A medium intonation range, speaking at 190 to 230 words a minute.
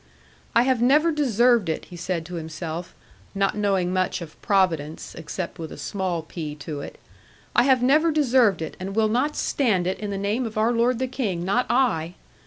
No: wide, 6.4 semitones; average, 195 wpm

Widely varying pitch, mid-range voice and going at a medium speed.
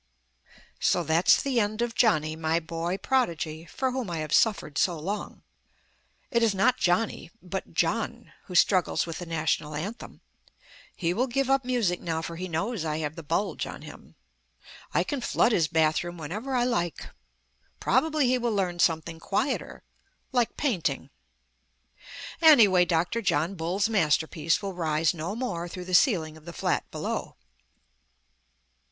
Yes: wide, 6.1 semitones; medium, 180 Hz; average, 155 wpm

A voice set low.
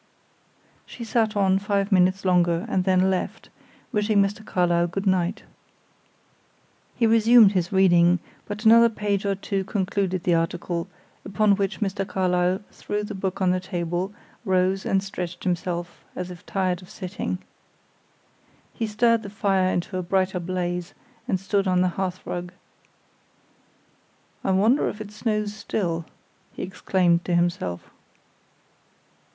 No: high, 190 Hz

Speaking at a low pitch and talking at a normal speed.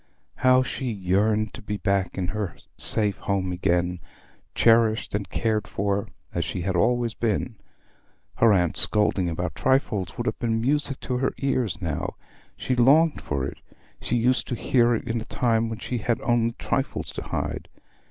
Yes: low, 110 Hz; average, 170 wpm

